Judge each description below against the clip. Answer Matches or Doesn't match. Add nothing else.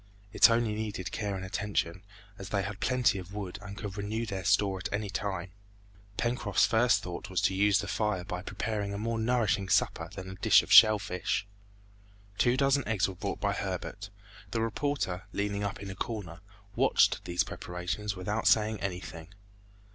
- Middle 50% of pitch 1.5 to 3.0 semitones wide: Matches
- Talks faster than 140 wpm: Matches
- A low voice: Matches